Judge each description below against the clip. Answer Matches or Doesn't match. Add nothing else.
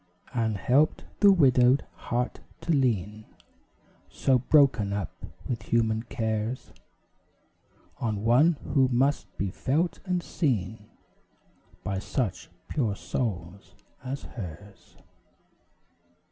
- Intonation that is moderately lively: Matches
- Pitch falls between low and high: Doesn't match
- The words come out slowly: Matches